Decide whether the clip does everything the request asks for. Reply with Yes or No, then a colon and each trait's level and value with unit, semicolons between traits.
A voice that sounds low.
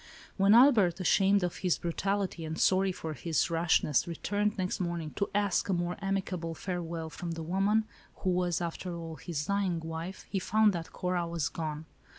No: medium, 175 Hz